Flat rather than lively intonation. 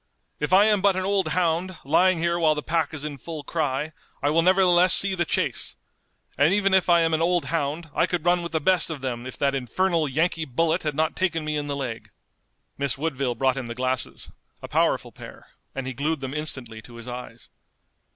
No: average, 4.2 semitones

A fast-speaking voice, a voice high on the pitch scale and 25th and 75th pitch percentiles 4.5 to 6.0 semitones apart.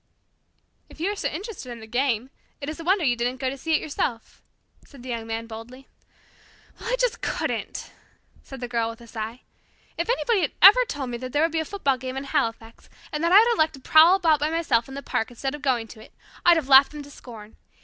Yes: fast, 245 wpm; very high, 270 Hz; average, 5.3 semitones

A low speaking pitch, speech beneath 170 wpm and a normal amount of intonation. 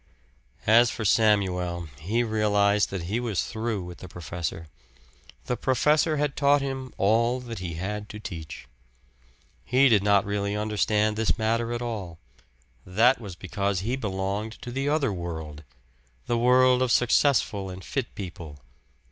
Yes: low, 105 Hz; average, 150 wpm; average, 4.2 semitones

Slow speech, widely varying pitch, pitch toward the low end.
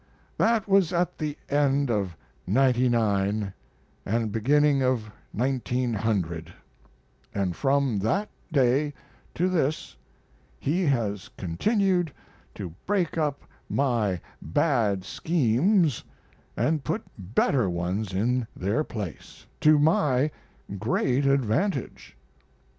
Yes: slow, 95 wpm; wide, 6.3 semitones; low, 130 Hz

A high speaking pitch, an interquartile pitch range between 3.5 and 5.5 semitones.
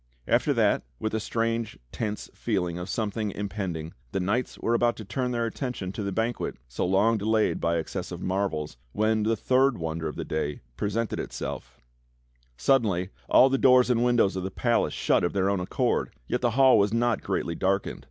No: low, 105 Hz; average, 4.1 semitones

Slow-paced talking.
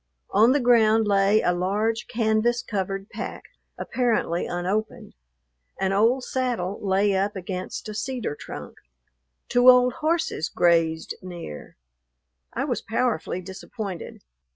Yes: slow, 120 wpm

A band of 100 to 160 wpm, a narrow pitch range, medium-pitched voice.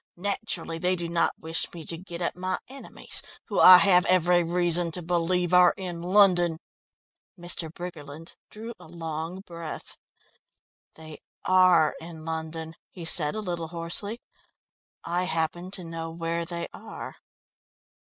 Yes: average, 145 wpm; narrow, 1.7 semitones; medium, 170 Hz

